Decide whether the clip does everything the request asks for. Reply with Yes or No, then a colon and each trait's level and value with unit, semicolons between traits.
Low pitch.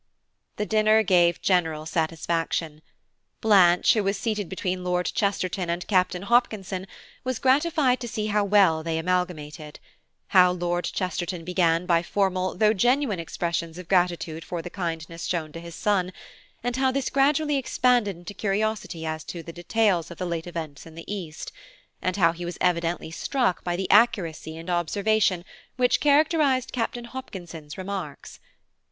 No: medium, 180 Hz